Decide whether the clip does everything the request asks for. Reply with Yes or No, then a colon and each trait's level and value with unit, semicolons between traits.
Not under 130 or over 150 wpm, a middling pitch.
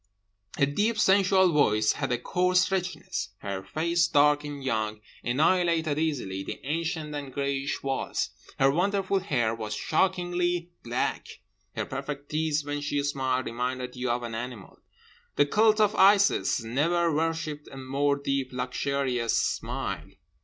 Yes: average, 140 wpm; medium, 145 Hz